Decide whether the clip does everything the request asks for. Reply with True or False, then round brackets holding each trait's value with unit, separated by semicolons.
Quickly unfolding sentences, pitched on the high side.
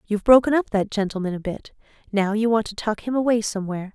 True (230 wpm; 215 Hz)